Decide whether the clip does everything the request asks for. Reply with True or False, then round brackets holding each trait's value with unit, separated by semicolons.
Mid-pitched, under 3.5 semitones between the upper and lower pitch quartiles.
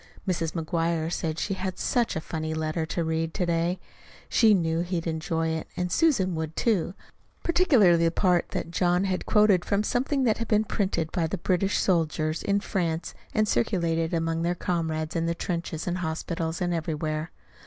True (170 Hz; 2.7 semitones)